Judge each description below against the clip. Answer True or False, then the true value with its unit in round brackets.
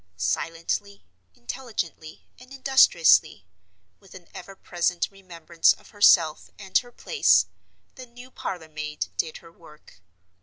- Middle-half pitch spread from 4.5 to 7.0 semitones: True (5.1 semitones)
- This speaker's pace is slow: True (110 wpm)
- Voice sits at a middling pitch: True (170 Hz)